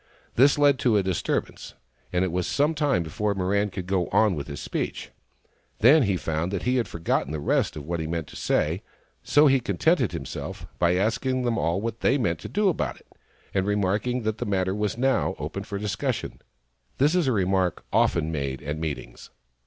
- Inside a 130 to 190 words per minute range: No, fast, 205 wpm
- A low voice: Yes, low, 100 Hz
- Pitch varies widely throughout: Yes, wide, 6.2 semitones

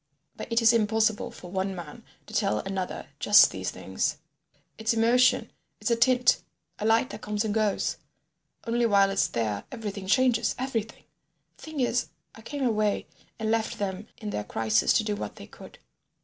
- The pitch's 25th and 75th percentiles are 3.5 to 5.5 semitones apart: No, average, 2.8 semitones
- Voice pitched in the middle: No, high, 220 Hz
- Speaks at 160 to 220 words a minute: Yes, average, 175 wpm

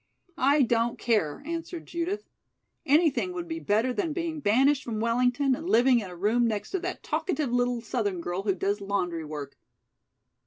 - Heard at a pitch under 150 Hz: No, high, 245 Hz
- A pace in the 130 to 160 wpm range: No, average, 170 wpm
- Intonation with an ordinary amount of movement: No, wide, 7.2 semitones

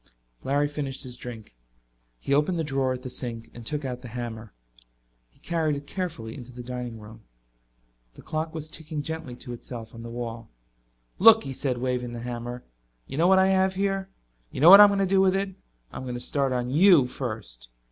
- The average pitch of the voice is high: No, low, 130 Hz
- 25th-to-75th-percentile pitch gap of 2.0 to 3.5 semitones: No, average, 5.0 semitones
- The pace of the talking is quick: Yes, fast, 210 wpm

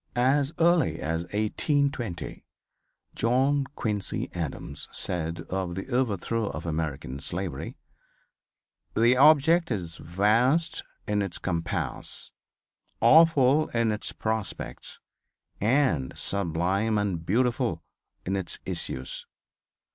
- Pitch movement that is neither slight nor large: No, wide, 7.1 semitones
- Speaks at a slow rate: Yes, slow, 95 wpm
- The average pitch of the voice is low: Yes, low, 105 Hz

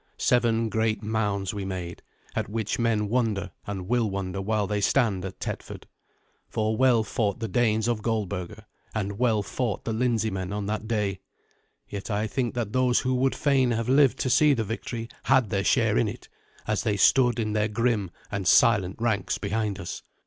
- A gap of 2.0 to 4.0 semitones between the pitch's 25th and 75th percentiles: Yes, average, 2.7 semitones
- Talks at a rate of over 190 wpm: No, average, 185 wpm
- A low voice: Yes, low, 110 Hz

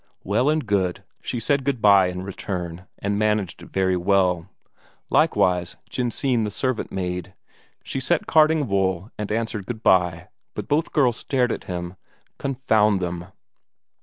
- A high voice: No, low, 100 Hz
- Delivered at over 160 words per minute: No, average, 150 wpm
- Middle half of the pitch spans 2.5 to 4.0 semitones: No, average, 5.2 semitones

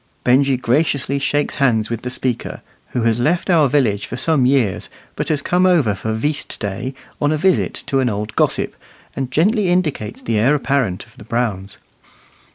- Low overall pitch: Yes, low, 130 Hz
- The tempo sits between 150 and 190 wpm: Yes, average, 180 wpm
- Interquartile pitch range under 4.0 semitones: No, average, 4.7 semitones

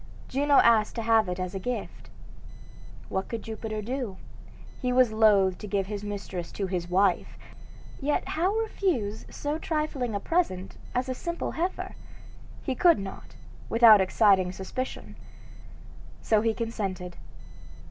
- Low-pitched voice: No, high, 220 Hz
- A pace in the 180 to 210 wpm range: No, average, 140 wpm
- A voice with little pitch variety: No, average, 4.9 semitones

